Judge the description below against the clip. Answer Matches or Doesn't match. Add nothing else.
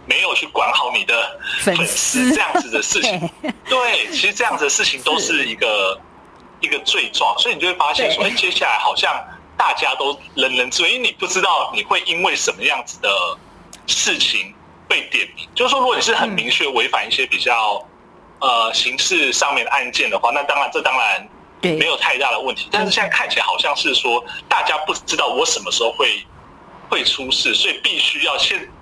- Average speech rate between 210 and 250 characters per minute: Doesn't match